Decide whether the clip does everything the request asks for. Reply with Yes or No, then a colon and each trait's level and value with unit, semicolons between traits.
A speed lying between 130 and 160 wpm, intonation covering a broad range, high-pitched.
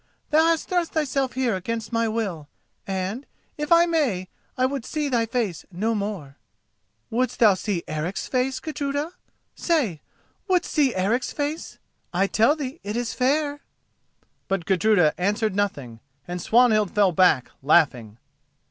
Yes: average, 140 wpm; wide, 7.0 semitones; high, 225 Hz